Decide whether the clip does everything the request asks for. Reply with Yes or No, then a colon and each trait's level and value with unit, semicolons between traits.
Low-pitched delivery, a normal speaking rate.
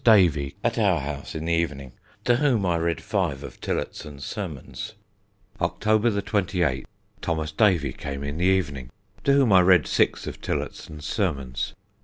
Yes: very low, 85 Hz; average, 160 wpm